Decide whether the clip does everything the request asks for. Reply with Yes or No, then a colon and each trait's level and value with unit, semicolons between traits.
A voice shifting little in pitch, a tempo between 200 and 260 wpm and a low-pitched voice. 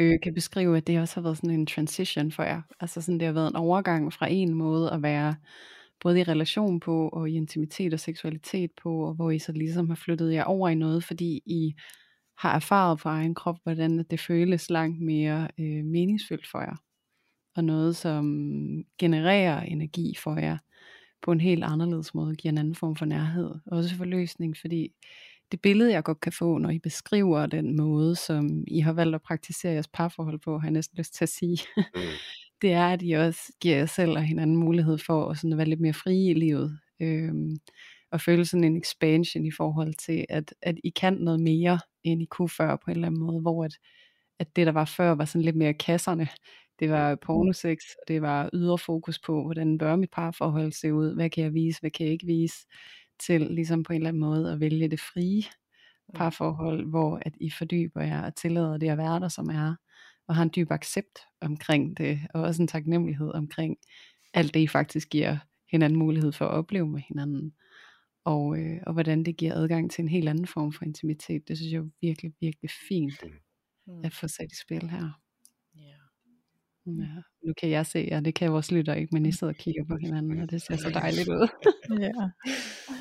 No: narrow, 1.6 semitones; average, 210 wpm; medium, 165 Hz